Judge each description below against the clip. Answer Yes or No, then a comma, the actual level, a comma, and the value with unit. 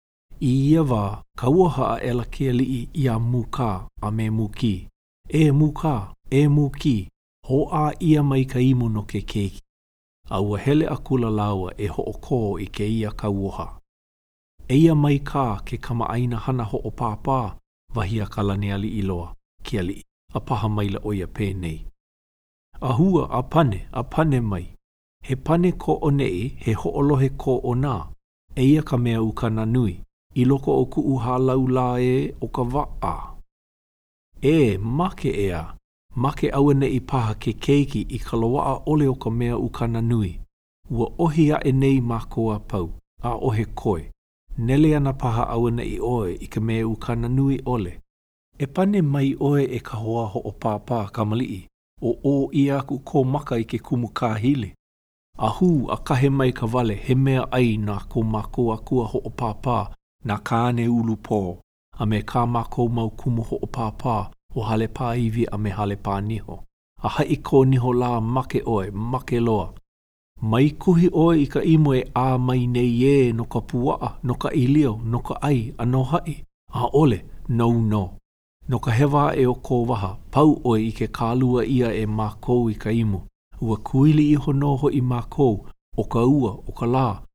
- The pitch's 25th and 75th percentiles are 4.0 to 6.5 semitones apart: Yes, average, 4.3 semitones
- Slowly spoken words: No, average, 185 wpm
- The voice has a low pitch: Yes, low, 120 Hz